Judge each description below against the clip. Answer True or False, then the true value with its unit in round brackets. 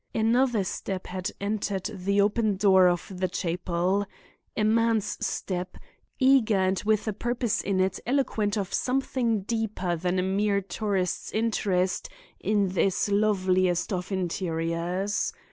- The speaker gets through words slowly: True (125 wpm)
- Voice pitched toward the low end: False (200 Hz)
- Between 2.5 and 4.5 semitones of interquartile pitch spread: True (2.8 semitones)